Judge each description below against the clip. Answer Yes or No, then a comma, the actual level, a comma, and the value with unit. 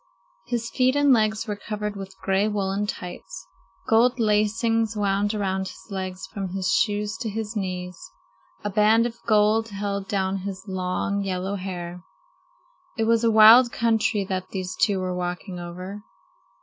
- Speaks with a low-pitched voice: No, high, 205 Hz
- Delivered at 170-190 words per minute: No, average, 155 wpm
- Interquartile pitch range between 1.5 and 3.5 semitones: Yes, average, 2.7 semitones